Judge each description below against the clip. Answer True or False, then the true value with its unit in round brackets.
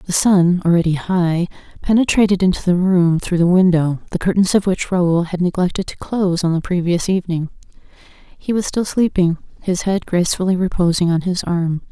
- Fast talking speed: False (175 wpm)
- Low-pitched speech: False (180 Hz)